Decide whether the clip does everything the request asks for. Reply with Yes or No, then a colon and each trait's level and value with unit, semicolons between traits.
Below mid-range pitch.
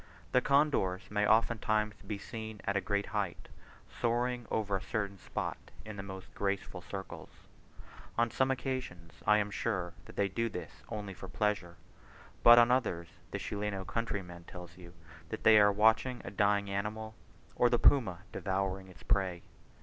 Yes: low, 100 Hz